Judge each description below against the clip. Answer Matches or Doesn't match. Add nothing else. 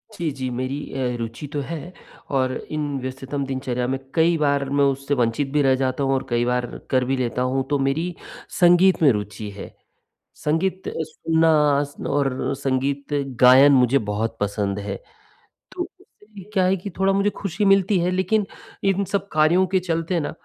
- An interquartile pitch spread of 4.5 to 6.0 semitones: Matches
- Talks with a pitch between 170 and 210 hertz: Doesn't match